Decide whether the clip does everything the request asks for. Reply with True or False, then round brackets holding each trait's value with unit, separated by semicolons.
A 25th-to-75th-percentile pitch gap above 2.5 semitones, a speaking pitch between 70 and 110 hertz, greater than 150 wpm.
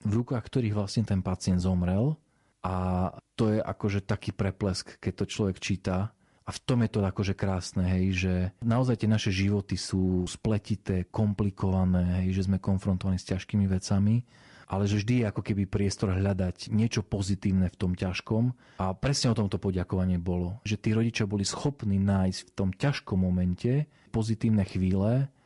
True (2.9 semitones; 100 Hz; 165 wpm)